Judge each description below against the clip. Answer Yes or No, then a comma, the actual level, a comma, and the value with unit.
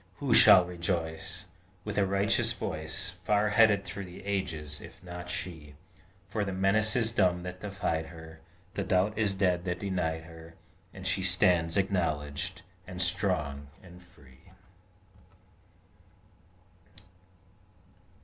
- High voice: No, very low, 90 Hz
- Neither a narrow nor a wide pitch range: Yes, average, 3.0 semitones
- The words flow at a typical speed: No, slow, 125 wpm